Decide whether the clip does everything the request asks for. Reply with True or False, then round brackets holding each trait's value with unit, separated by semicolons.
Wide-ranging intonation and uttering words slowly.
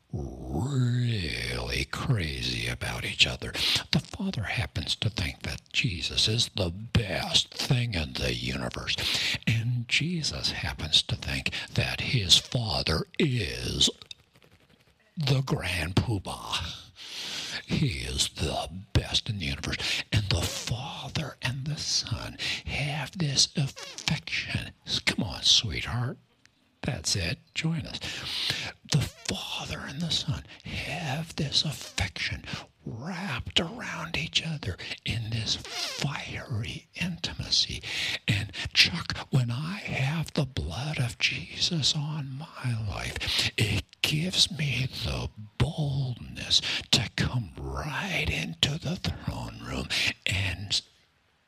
True (7.8 semitones; 110 wpm)